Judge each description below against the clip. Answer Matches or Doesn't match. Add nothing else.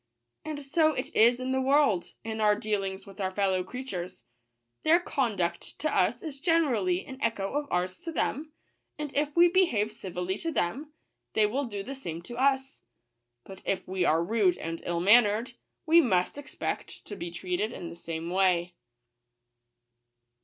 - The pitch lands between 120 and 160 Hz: Doesn't match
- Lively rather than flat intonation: Matches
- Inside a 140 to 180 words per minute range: Matches